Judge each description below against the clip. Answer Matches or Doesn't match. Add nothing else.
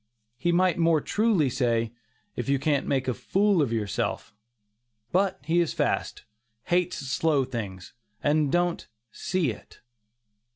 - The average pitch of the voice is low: Doesn't match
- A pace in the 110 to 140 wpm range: Matches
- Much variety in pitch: Matches